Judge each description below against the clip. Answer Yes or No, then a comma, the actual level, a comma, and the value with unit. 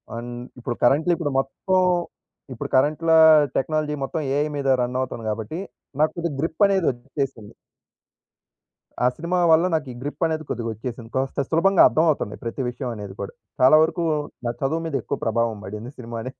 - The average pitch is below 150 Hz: Yes, low, 135 Hz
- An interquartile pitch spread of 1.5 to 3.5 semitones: No, average, 5.2 semitones